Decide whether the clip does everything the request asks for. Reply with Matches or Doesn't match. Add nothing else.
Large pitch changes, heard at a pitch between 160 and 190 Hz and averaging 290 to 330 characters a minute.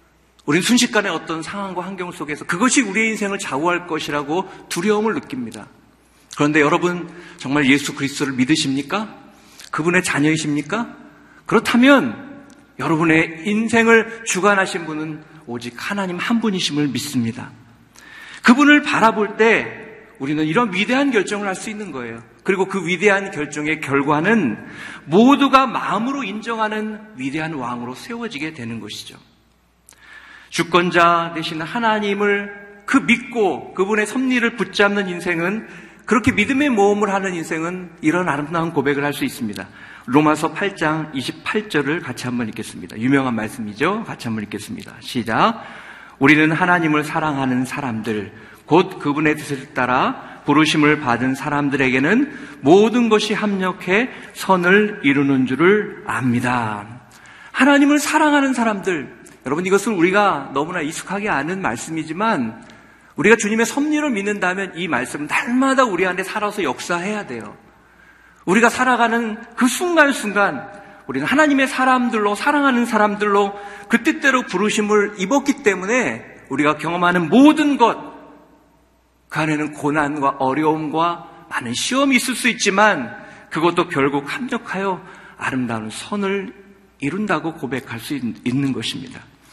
Matches